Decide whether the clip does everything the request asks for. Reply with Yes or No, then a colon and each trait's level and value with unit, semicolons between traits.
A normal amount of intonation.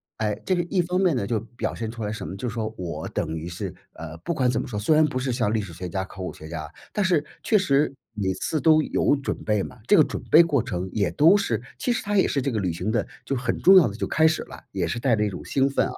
No: wide, 8.1 semitones